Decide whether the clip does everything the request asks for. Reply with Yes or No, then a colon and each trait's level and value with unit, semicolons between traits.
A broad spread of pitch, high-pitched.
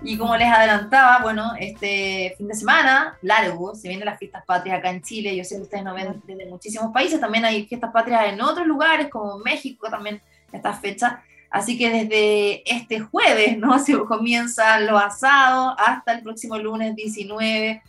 No: average, 2.9 semitones; high, 220 Hz